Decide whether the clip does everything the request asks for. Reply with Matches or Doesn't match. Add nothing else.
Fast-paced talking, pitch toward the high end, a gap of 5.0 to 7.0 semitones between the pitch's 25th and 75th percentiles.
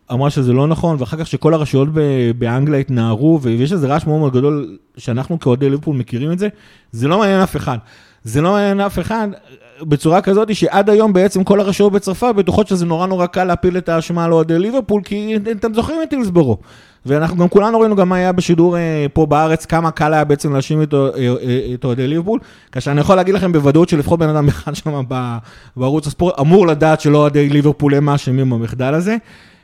Doesn't match